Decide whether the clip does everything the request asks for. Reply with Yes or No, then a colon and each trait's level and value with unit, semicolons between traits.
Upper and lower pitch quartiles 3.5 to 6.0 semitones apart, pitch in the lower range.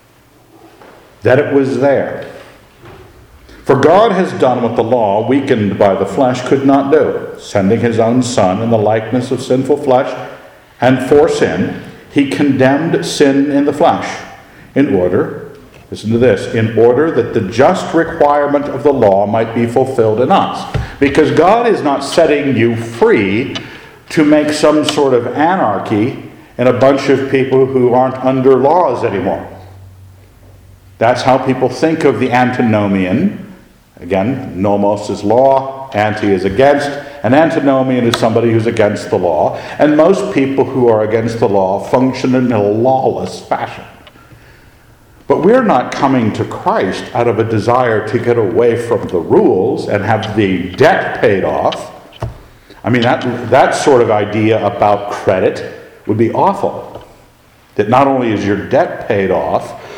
Yes: average, 4.4 semitones; low, 125 Hz